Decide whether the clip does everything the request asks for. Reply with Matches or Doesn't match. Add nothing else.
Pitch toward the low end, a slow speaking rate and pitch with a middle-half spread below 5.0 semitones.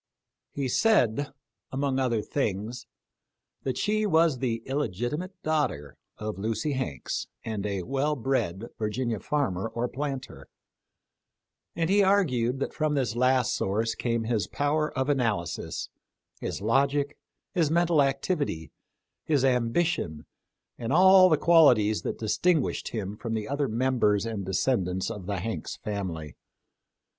Doesn't match